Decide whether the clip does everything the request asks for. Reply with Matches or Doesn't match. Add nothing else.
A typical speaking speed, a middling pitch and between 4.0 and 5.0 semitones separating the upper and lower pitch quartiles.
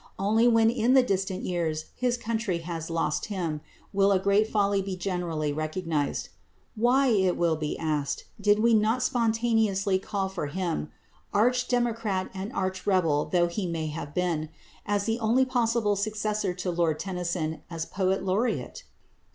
Doesn't match